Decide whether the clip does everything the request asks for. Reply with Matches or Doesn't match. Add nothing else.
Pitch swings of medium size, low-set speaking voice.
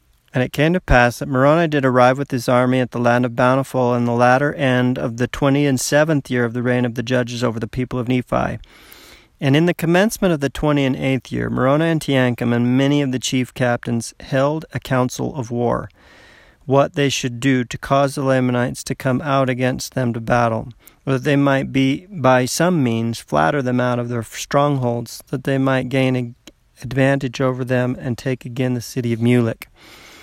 Doesn't match